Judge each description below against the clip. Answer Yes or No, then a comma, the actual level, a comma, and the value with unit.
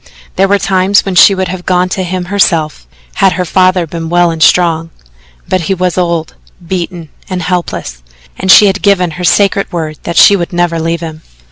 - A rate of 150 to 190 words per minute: No, average, 200 wpm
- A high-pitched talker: No, medium, 180 Hz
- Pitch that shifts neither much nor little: No, narrow, 2.1 semitones